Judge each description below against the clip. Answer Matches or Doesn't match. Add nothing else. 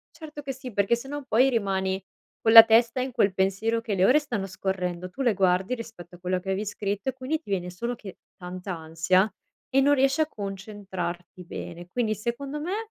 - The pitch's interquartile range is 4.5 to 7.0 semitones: Matches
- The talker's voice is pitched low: Doesn't match